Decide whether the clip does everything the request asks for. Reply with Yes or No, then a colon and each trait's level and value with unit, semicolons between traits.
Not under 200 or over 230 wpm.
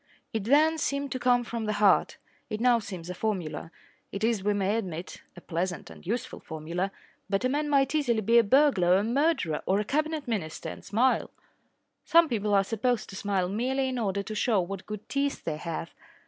Yes: fast, 205 wpm